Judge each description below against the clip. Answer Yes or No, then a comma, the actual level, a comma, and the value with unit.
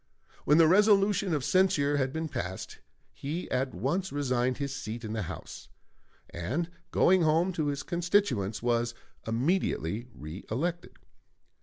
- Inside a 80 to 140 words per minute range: Yes, slow, 135 wpm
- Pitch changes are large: Yes, wide, 6.8 semitones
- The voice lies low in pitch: No, medium, 145 Hz